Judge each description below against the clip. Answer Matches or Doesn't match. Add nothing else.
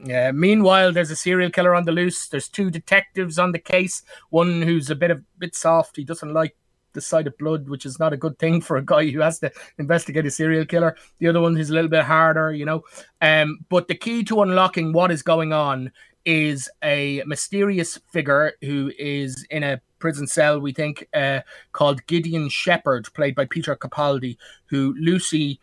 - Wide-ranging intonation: Doesn't match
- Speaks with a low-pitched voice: Doesn't match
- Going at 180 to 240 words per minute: Matches